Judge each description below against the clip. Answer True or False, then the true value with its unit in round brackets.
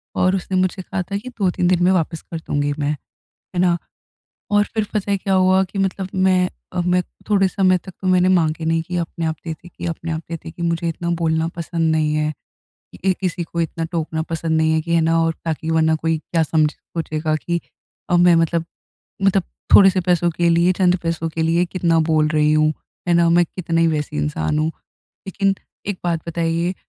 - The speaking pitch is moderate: True (170 Hz)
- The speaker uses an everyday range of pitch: False (2.3 semitones)